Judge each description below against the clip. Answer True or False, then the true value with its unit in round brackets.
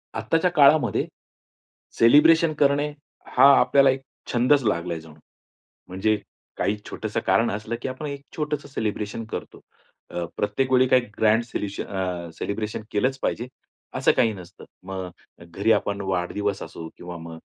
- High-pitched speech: False (110 Hz)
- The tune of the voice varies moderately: False (5.8 semitones)